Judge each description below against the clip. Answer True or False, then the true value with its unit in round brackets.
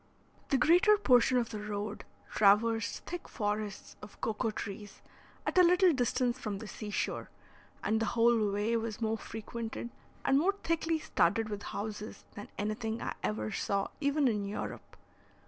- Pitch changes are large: False (3.3 semitones)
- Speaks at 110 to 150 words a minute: False (160 wpm)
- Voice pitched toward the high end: True (225 Hz)